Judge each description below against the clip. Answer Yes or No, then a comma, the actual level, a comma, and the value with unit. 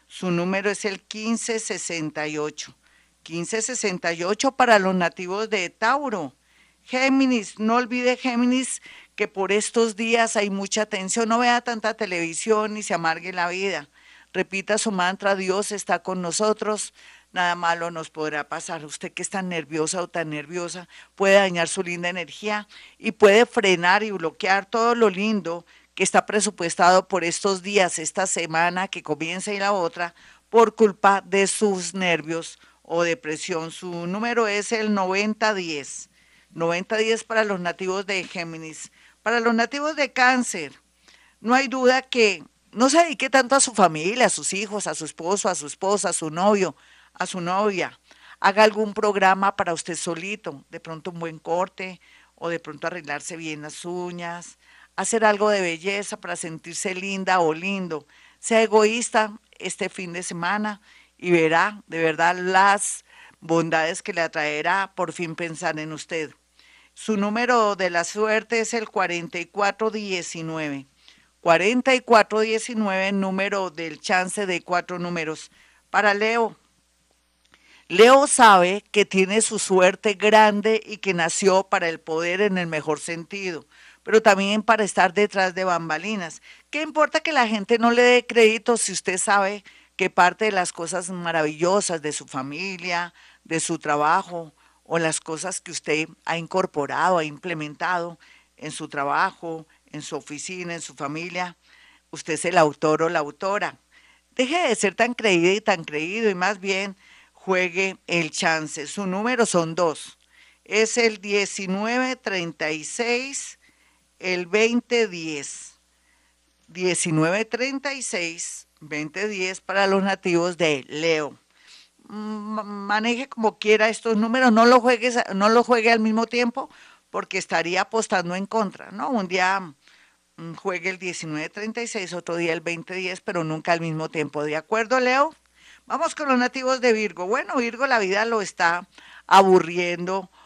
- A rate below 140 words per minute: No, average, 145 wpm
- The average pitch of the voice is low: No, high, 190 Hz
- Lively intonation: No, average, 4.3 semitones